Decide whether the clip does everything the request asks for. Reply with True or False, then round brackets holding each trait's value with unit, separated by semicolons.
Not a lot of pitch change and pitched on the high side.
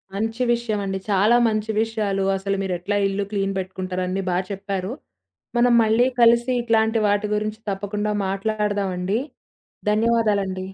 True (2.3 semitones; 205 Hz)